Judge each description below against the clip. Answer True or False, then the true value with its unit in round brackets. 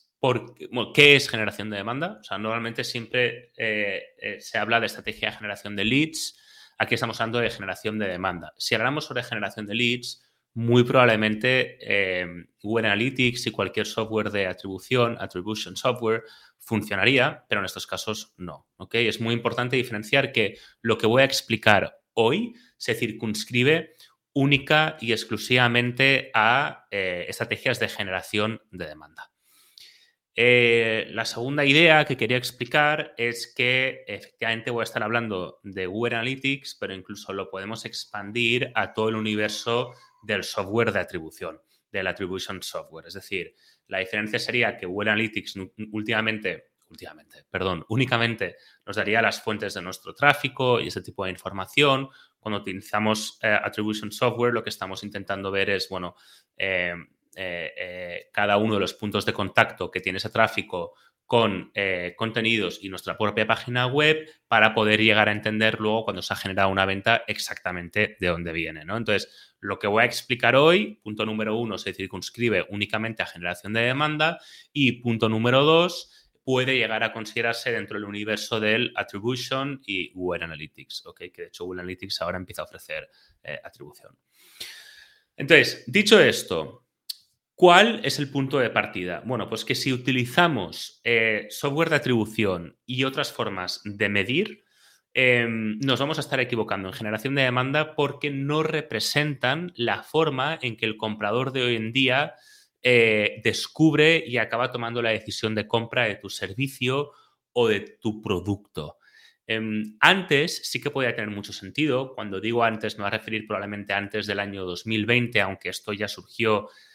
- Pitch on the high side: False (115 Hz)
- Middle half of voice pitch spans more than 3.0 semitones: True (4.0 semitones)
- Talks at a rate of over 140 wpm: True (160 wpm)